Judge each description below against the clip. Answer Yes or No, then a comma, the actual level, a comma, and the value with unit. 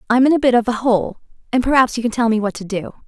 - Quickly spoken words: Yes, fast, 315 wpm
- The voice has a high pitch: Yes, high, 235 Hz